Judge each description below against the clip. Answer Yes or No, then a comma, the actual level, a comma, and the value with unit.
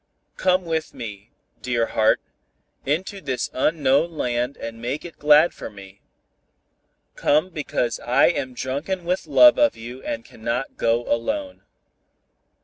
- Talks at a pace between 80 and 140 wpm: Yes, slow, 135 wpm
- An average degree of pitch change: No, wide, 6.2 semitones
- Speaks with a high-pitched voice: No, low, 135 Hz